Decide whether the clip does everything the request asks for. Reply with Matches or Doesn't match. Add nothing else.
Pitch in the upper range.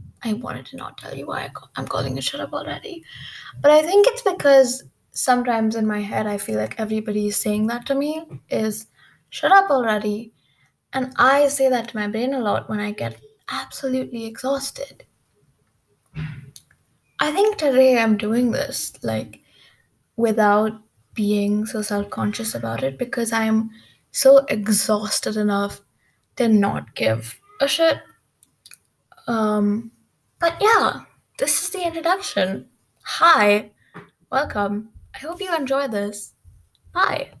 Matches